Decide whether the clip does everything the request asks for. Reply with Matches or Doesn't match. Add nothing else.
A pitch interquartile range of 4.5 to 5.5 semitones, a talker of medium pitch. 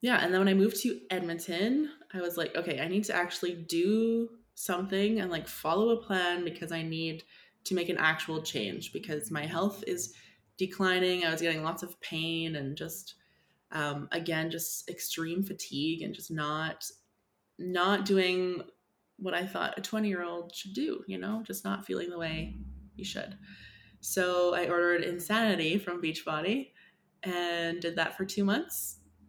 Doesn't match